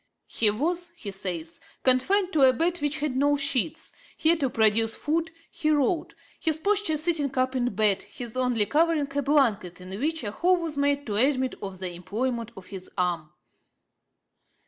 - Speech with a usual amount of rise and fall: No, wide, 6.5 semitones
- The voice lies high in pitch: Yes, very high, 260 Hz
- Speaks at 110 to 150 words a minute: No, average, 175 wpm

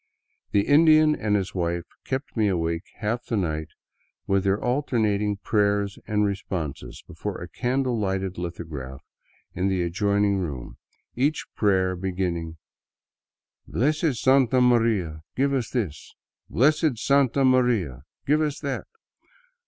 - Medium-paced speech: No, slow, 130 wpm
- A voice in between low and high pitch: No, low, 105 Hz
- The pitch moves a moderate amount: No, wide, 5.9 semitones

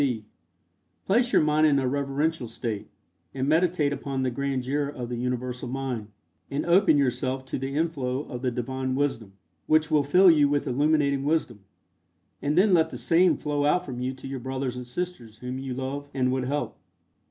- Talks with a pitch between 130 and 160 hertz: Yes, low, 135 Hz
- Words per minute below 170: No, average, 185 wpm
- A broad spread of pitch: No, average, 2.9 semitones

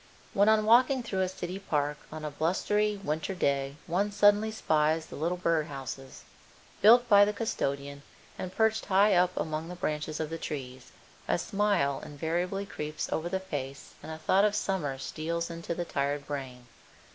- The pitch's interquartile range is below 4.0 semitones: No, wide, 5.4 semitones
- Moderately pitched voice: Yes, medium, 170 Hz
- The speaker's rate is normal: Yes, average, 175 wpm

